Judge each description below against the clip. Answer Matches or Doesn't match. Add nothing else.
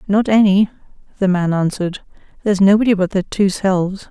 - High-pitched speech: Matches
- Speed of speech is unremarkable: Matches